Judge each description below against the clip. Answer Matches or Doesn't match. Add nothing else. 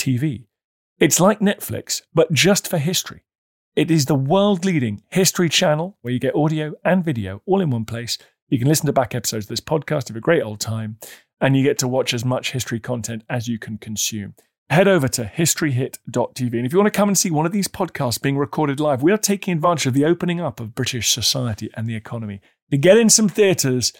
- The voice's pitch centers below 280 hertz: Matches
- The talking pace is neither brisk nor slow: Doesn't match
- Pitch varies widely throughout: Matches